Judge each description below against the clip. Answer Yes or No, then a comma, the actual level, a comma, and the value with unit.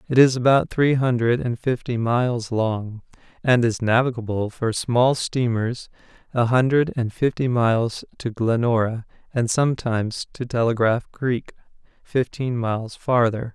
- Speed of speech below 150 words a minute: Yes, slow, 135 wpm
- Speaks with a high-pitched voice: No, low, 120 Hz